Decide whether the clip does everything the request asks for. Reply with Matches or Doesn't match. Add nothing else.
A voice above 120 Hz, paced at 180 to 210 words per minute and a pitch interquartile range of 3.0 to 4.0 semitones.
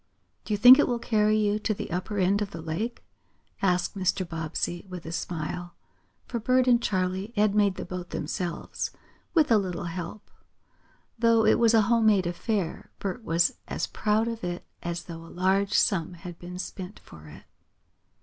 Matches